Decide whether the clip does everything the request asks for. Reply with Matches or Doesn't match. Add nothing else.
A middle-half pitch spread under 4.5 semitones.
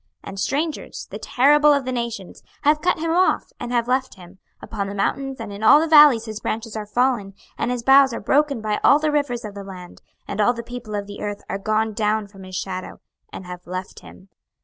Doesn't match